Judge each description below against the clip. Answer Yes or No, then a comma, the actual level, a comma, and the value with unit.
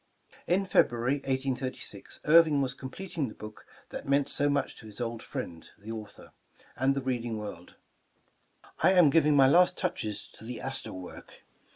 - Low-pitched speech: Yes, low, 130 Hz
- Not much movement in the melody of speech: No, average, 4.2 semitones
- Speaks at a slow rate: No, average, 165 wpm